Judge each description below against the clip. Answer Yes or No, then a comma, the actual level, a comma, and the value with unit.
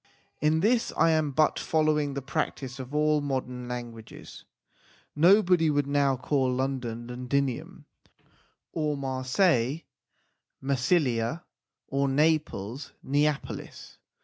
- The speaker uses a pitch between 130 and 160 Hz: Yes, medium, 140 Hz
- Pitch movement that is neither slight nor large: Yes, average, 3.2 semitones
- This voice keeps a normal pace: No, slow, 100 wpm